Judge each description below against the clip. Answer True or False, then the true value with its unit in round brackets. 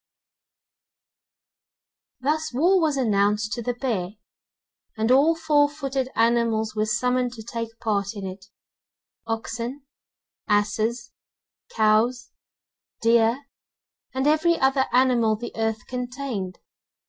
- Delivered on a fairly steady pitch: False (3.4 semitones)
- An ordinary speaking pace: False (105 wpm)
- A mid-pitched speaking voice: False (235 Hz)